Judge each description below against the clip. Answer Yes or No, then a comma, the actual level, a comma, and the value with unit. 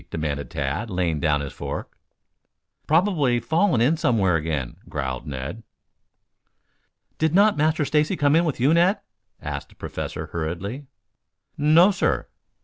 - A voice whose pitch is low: Yes, low, 120 Hz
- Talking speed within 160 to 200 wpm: No, slow, 135 wpm